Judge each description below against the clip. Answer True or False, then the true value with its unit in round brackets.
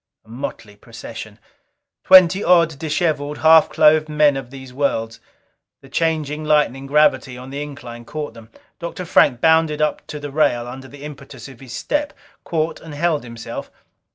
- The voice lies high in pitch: False (145 Hz)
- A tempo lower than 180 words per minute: True (155 wpm)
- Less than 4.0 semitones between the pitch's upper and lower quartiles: True (3.3 semitones)